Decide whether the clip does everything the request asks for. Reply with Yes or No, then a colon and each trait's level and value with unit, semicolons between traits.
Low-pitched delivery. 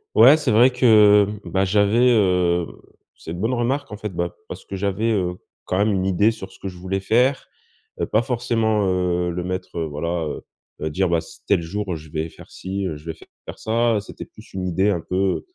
Yes: very low, 95 Hz